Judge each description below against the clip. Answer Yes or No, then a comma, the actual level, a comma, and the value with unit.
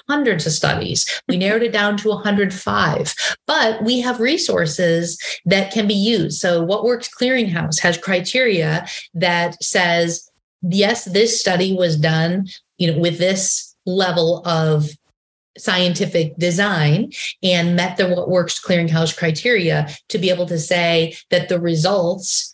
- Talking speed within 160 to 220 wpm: No, average, 140 wpm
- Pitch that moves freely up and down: No, average, 3.4 semitones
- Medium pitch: Yes, medium, 180 Hz